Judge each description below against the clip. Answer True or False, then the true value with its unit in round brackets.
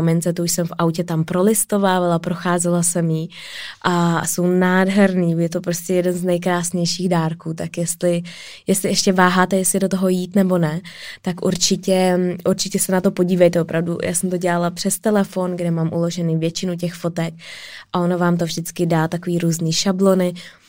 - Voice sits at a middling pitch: True (180 Hz)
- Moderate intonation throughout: False (1.5 semitones)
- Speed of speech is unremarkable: False (175 wpm)